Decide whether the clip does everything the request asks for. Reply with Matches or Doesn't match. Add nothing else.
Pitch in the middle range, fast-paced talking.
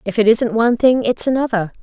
Doesn't match